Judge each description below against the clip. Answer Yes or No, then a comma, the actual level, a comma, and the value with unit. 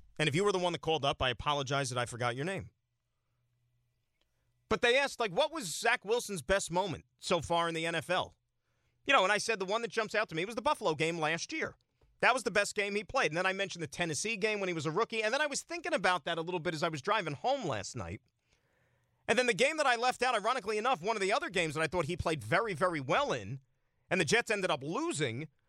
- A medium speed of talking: No, fast, 270 wpm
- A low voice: No, medium, 180 Hz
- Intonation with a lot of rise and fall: Yes, wide, 7.1 semitones